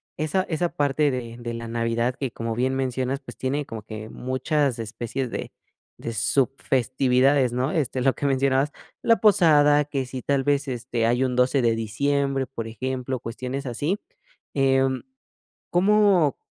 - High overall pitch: No, low, 130 Hz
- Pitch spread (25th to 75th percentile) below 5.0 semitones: Yes, average, 2.9 semitones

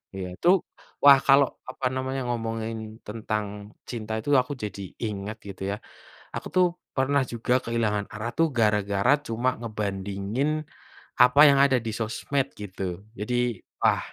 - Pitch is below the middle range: Yes, low, 115 Hz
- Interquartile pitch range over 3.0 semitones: Yes, average, 3.9 semitones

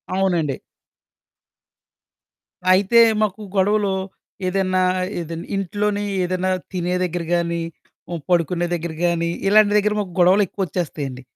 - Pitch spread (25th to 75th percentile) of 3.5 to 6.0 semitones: No, narrow, 2.5 semitones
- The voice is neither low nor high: Yes, medium, 180 Hz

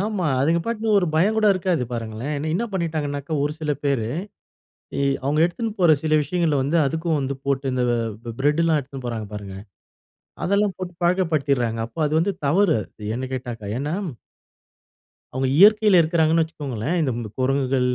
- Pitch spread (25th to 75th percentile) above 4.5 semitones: Yes, average, 5.0 semitones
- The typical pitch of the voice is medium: Yes, medium, 150 Hz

